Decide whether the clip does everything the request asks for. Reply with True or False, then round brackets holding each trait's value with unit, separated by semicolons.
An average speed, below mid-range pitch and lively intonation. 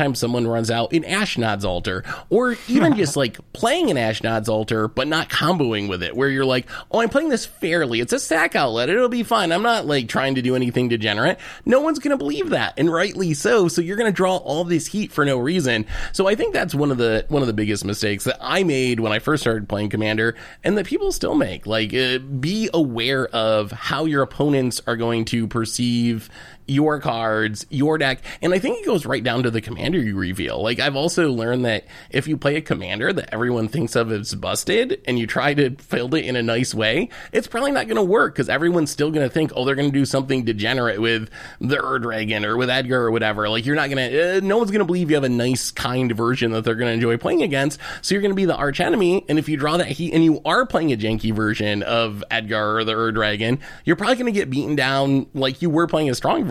False (245 wpm; 130 Hz; 6.0 semitones)